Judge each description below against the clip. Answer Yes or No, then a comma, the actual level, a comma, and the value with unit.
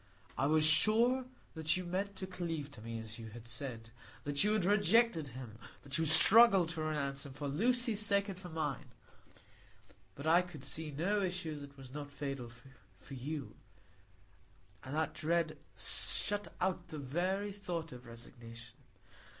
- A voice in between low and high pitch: Yes, medium, 155 Hz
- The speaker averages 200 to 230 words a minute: No, average, 165 wpm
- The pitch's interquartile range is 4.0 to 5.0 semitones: No, wide, 5.4 semitones